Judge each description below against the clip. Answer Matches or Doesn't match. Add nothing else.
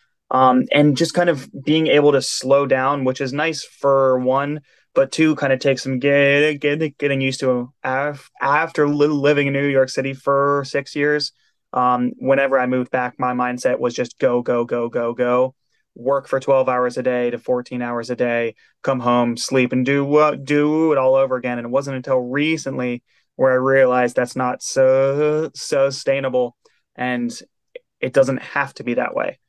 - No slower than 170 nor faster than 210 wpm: Matches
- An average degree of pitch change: Doesn't match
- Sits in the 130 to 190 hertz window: Matches